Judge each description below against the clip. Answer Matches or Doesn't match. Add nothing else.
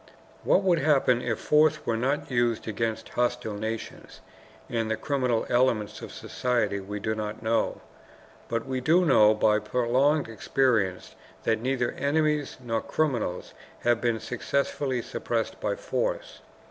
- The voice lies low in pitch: Matches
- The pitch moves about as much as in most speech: Matches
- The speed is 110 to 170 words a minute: Matches